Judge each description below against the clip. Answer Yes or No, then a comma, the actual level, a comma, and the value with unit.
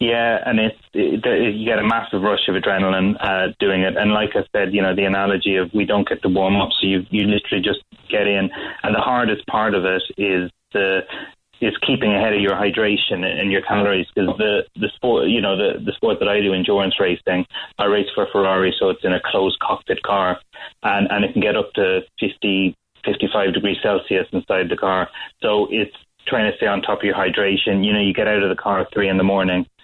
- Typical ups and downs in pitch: No, narrow, 1.4 semitones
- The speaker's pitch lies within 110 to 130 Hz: No, low, 100 Hz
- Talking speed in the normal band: No, fast, 235 wpm